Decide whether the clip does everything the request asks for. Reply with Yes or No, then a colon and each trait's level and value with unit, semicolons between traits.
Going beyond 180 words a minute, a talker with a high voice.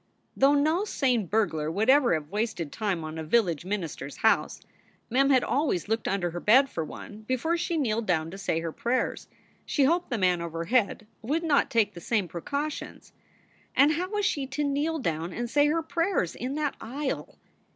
Yes: average, 195 wpm; high, 235 Hz